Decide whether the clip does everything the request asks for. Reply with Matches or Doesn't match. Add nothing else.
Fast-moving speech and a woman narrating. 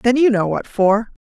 Matches